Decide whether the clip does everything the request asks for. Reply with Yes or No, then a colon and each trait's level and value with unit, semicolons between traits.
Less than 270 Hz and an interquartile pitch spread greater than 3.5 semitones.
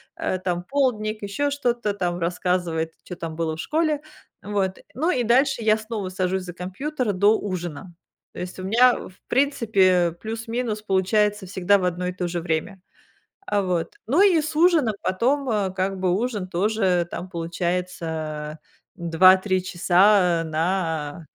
Yes: high, 190 Hz; average, 3.9 semitones